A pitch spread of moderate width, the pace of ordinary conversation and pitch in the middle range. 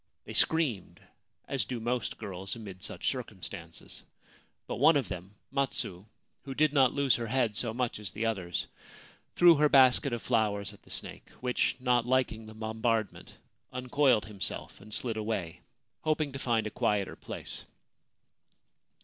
No: average, 3.8 semitones; average, 160 wpm; low, 115 Hz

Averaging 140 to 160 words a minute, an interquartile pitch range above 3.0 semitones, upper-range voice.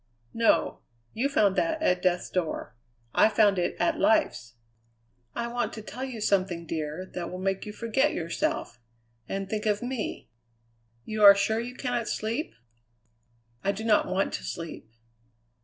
Yes: average, 155 wpm; average, 4.4 semitones; high, 210 Hz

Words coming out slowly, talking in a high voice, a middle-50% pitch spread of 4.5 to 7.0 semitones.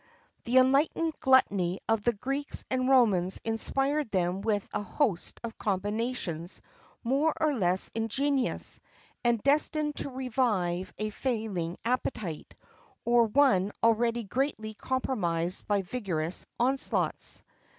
Yes: slow, 120 wpm; high, 230 Hz; average, 5.2 semitones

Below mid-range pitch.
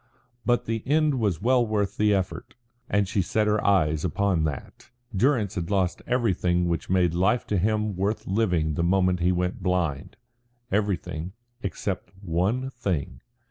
Yes: very low, 95 Hz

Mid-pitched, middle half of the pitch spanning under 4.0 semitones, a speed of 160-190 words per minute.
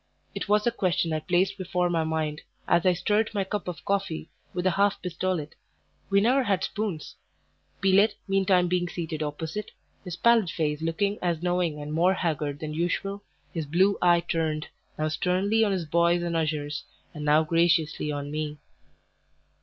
Yes: medium, 175 Hz; average, 3.6 semitones; average, 170 wpm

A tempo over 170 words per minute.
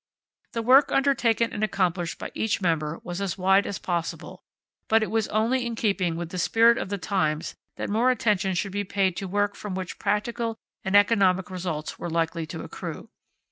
Yes: average, 190 wpm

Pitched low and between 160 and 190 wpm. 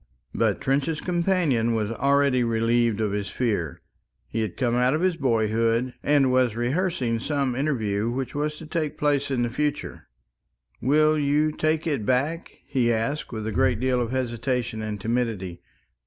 Yes: low, 125 Hz; average, 165 wpm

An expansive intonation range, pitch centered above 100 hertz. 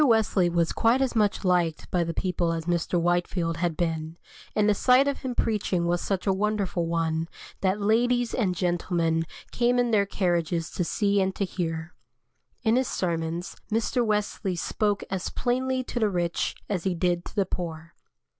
No: average, 3.9 semitones; medium, 185 Hz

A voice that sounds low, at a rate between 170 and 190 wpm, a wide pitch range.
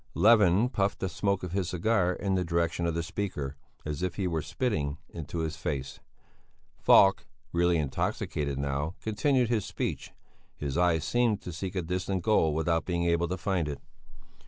No: very low, 85 Hz; average, 175 wpm; average, 3.4 semitones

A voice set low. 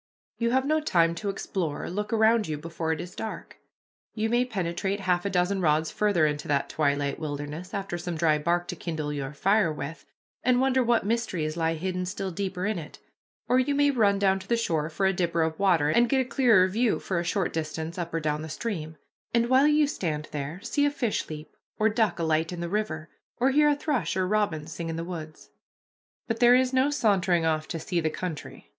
No: medium, 180 Hz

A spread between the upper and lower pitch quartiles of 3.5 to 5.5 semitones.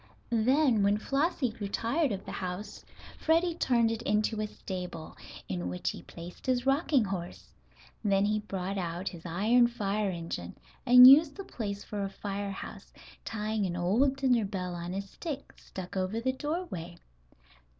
Yes: average, 5.1 semitones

